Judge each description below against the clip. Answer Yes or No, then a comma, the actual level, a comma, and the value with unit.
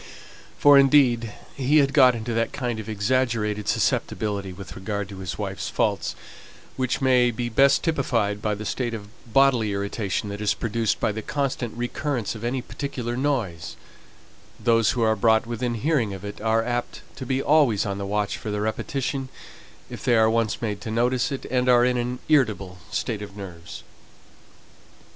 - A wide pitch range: No, average, 3.6 semitones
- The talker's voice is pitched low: Yes, low, 115 Hz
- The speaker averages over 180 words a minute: No, average, 175 wpm